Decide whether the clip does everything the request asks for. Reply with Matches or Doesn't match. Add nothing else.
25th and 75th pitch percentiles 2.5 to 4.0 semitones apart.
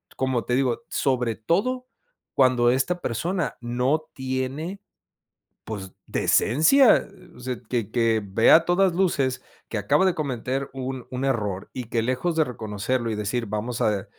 Doesn't match